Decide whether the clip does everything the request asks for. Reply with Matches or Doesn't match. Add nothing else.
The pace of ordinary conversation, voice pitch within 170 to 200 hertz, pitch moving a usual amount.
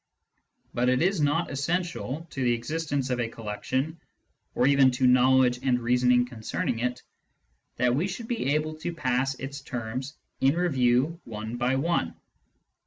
Doesn't match